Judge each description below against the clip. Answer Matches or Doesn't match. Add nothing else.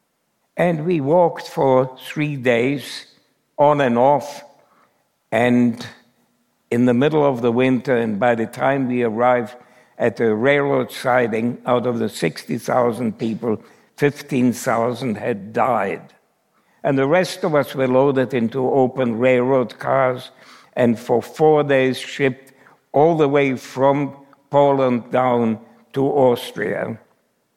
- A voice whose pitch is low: Matches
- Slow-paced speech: Matches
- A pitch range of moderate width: Doesn't match